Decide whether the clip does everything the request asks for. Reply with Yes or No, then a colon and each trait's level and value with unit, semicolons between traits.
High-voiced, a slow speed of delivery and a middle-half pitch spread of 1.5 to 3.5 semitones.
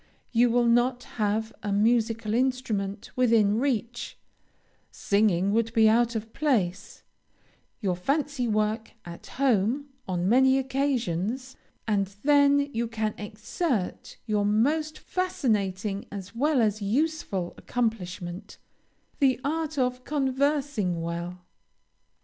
No: high, 230 Hz; slow, 110 wpm; average, 4.5 semitones